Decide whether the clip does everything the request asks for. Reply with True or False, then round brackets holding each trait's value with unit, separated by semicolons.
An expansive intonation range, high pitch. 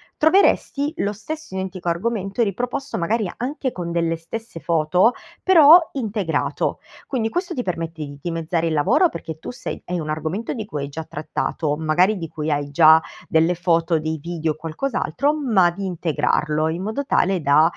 False (6.2 semitones; 175 Hz)